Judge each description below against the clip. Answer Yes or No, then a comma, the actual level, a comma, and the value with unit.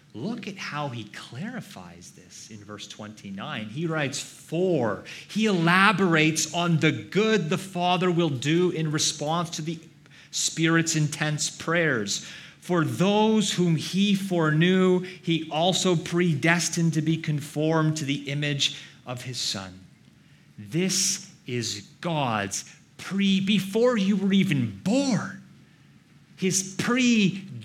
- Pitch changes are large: No, average, 4.1 semitones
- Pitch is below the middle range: No, medium, 165 Hz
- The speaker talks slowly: Yes, slow, 120 wpm